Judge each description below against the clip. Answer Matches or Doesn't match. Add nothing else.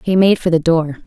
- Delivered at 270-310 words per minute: Matches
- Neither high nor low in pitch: Matches